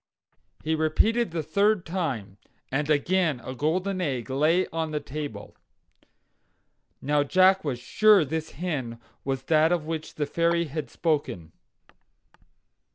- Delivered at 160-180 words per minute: No, slow, 135 wpm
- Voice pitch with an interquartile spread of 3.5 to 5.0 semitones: Yes, average, 3.8 semitones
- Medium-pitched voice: Yes, medium, 155 Hz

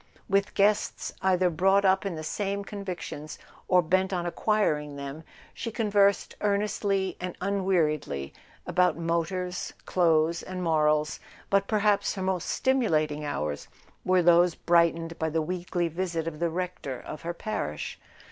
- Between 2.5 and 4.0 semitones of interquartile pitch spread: Yes, average, 3.5 semitones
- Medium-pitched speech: Yes, medium, 180 Hz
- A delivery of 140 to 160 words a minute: Yes, average, 150 wpm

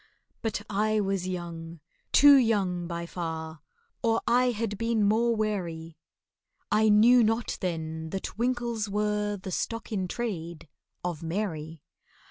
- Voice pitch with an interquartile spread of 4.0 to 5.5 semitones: Yes, average, 4.8 semitones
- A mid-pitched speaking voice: No, high, 205 Hz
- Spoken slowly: Yes, slow, 125 wpm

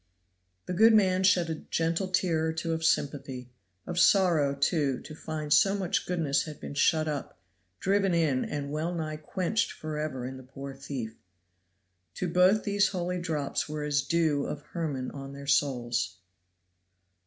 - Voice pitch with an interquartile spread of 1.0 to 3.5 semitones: No, average, 4.1 semitones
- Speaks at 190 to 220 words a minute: No, average, 165 wpm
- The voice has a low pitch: No, medium, 155 Hz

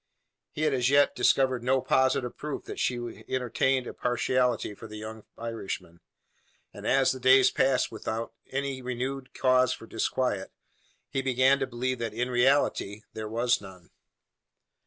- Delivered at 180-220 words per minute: No, average, 155 wpm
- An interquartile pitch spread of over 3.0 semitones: No, narrow, 2.4 semitones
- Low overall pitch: Yes, low, 125 Hz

